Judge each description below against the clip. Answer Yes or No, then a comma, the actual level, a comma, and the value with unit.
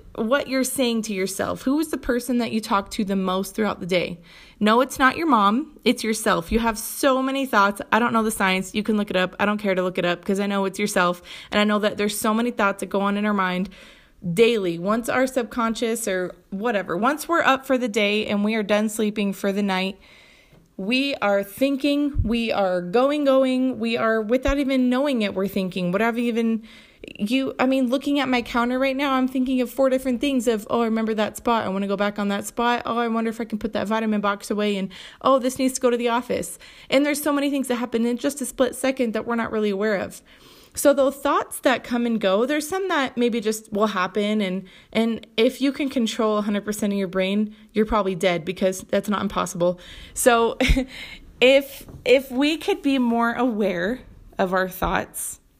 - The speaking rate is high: Yes, fast, 240 wpm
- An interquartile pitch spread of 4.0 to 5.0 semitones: Yes, average, 4.3 semitones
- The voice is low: No, high, 225 Hz